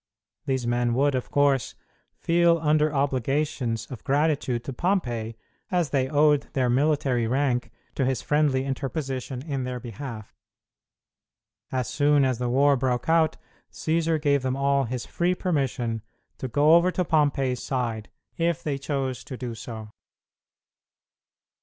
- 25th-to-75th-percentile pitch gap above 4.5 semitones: No, average, 3.2 semitones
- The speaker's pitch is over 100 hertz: Yes, low, 135 Hz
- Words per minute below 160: Yes, average, 140 wpm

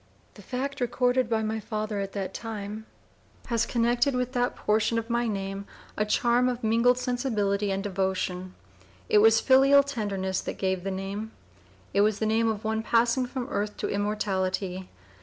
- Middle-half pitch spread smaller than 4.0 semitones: Yes, average, 3.3 semitones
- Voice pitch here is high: Yes, high, 220 Hz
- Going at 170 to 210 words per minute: Yes, average, 175 wpm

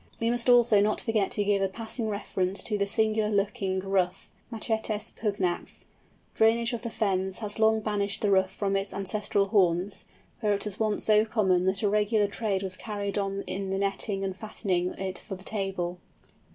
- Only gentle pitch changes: Yes, narrow, 2.0 semitones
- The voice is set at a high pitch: Yes, high, 205 Hz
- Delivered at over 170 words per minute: Yes, average, 185 wpm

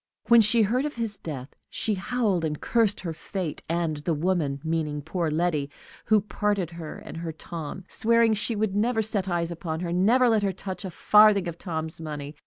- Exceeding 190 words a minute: Yes, average, 200 wpm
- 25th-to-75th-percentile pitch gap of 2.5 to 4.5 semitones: No, average, 4.9 semitones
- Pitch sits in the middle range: Yes, medium, 180 Hz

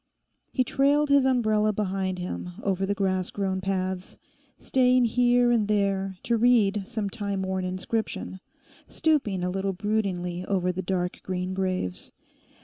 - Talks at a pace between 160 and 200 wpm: No, average, 140 wpm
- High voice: Yes, high, 195 Hz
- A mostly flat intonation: No, average, 3.2 semitones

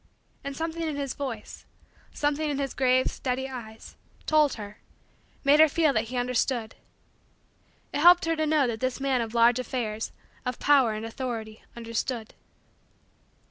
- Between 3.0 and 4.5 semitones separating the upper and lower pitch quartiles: Yes, average, 3.9 semitones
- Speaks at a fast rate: No, average, 155 wpm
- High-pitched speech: Yes, very high, 255 Hz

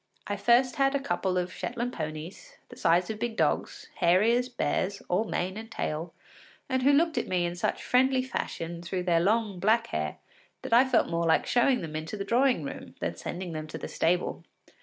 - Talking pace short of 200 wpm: No, fast, 205 wpm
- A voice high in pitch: Yes, high, 200 Hz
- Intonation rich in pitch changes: Yes, wide, 6.1 semitones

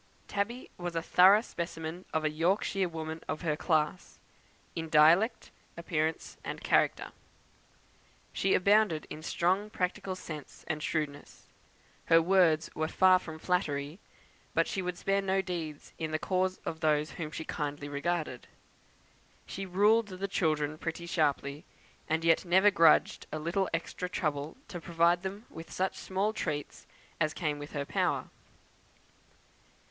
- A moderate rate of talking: Yes, average, 150 wpm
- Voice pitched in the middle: Yes, medium, 170 Hz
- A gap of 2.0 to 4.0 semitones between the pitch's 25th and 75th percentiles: Yes, average, 3.2 semitones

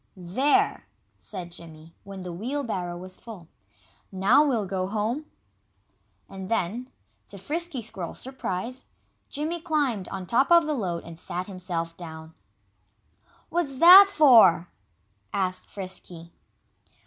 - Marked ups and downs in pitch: Yes, wide, 7.2 semitones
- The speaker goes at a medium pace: No, slow, 120 wpm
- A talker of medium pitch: No, high, 200 Hz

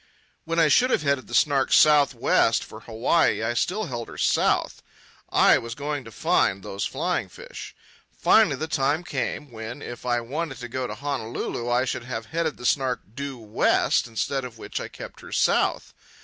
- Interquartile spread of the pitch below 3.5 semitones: No, average, 4.1 semitones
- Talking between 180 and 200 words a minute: Yes, average, 190 wpm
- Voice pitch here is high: No, low, 130 Hz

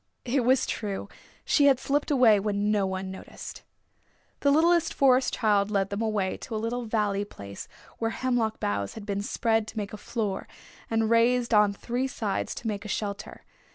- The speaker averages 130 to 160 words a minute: No, average, 185 wpm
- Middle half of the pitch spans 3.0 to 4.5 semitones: Yes, average, 3.4 semitones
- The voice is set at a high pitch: Yes, high, 220 Hz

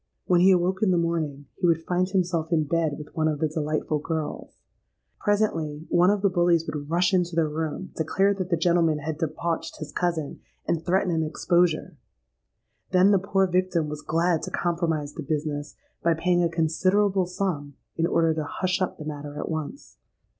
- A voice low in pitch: No, medium, 165 Hz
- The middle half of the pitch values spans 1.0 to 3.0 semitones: Yes, narrow, 2.6 semitones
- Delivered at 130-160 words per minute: No, average, 190 wpm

